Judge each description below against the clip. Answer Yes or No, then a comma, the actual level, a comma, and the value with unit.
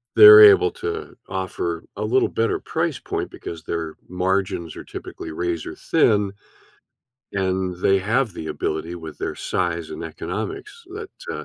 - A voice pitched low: Yes, very low, 95 Hz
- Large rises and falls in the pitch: Yes, wide, 8.1 semitones